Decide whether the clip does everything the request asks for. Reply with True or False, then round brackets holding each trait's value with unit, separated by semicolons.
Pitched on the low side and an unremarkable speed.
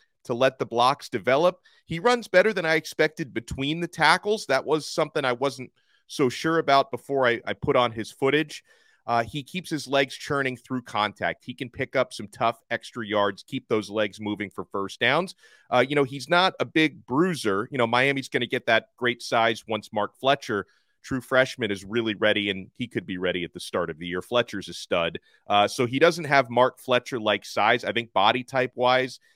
False (125 Hz; 215 wpm)